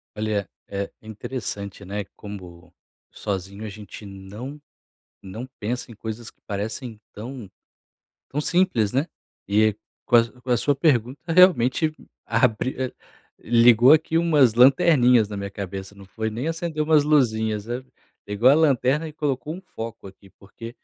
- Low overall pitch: Yes, low, 115 Hz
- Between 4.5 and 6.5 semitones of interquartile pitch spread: Yes, average, 4.8 semitones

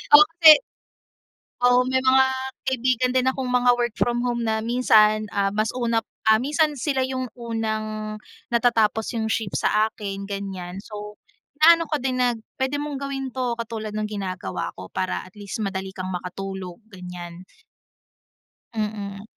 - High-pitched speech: Yes, high, 220 Hz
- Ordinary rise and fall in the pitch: Yes, average, 4.1 semitones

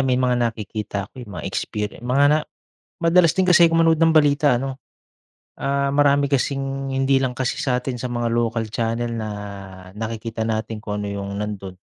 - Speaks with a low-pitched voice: Yes, low, 125 Hz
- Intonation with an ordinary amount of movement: Yes, average, 4.0 semitones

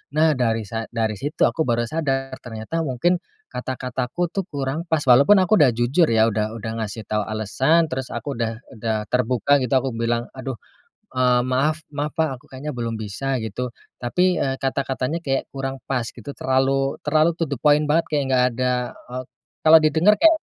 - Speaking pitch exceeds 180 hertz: No, low, 130 Hz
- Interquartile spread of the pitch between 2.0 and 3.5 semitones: No, average, 4.4 semitones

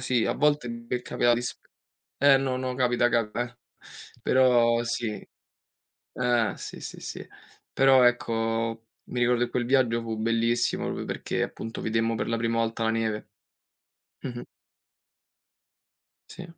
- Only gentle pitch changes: Yes, narrow, 1.6 semitones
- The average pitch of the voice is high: No, low, 120 Hz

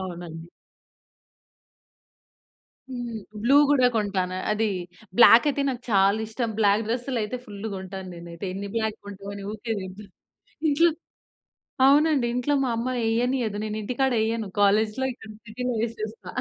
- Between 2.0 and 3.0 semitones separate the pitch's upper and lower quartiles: No, average, 3.5 semitones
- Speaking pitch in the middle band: No, high, 220 Hz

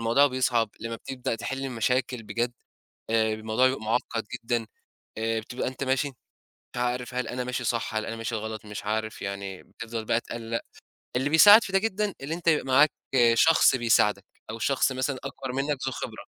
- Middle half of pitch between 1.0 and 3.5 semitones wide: Yes, average, 2.9 semitones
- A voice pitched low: Yes, low, 120 Hz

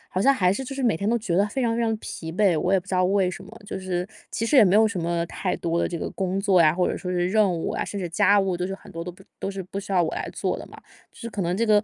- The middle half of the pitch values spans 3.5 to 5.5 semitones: No, average, 2.7 semitones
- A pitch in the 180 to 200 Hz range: Yes, high, 190 Hz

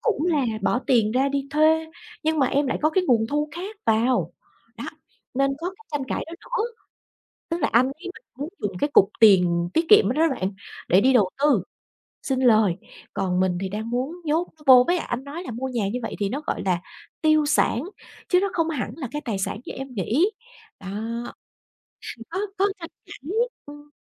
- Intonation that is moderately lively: No, wide, 6.1 semitones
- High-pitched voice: Yes, very high, 270 Hz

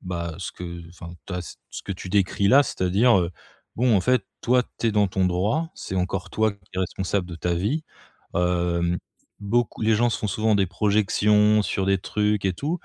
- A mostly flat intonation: No, average, 3.2 semitones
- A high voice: No, low, 100 Hz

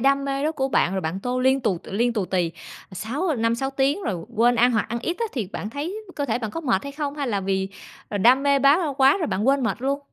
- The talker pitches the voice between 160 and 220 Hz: No, very high, 255 Hz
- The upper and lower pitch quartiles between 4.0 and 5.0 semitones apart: Yes, average, 4.7 semitones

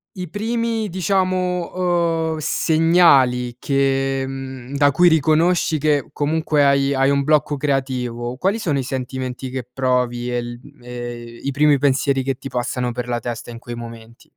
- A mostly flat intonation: No, average, 4.4 semitones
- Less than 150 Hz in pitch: Yes, low, 135 Hz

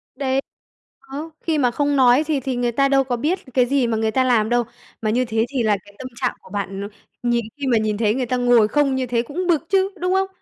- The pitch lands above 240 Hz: Yes, very high, 255 Hz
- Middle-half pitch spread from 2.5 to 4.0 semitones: Yes, average, 3.4 semitones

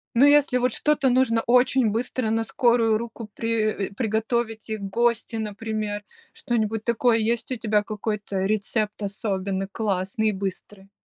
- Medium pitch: No, high, 220 Hz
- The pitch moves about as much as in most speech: No, narrow, 2.3 semitones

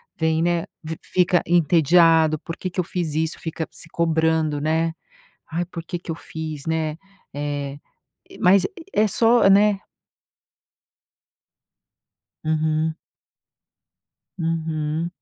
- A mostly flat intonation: Yes, narrow, 1.8 semitones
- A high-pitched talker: No, medium, 160 Hz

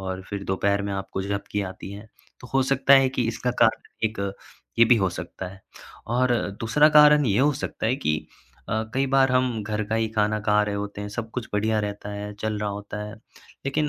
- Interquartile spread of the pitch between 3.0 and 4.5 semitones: Yes, average, 3.8 semitones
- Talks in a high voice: No, low, 110 Hz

